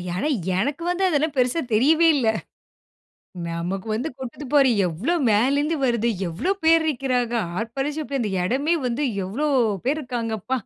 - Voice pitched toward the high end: Yes, very high, 265 Hz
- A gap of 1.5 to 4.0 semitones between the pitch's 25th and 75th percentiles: No, average, 4.8 semitones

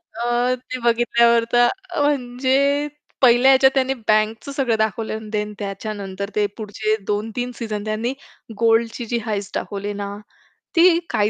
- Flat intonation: No, average, 3.0 semitones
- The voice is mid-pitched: No, high, 230 Hz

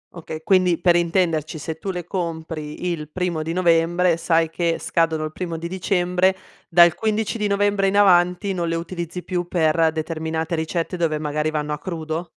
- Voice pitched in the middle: Yes, medium, 170 Hz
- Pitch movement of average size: No, narrow, 2.1 semitones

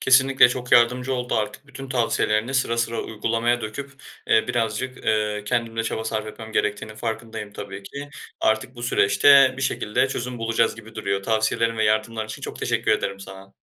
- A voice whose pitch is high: No, low, 115 Hz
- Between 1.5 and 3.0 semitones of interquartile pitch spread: Yes, narrow, 2.5 semitones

